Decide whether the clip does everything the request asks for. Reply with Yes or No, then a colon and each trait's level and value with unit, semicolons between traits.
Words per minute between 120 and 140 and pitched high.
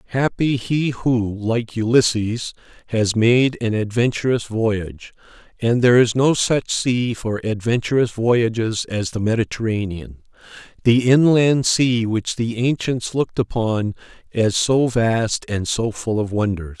No: slow, 135 wpm; low, 115 Hz